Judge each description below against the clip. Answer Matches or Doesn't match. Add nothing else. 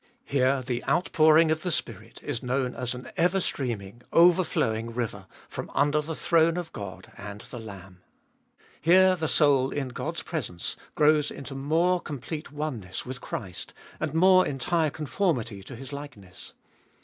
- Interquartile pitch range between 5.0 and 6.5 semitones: Matches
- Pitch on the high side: Doesn't match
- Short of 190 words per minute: Matches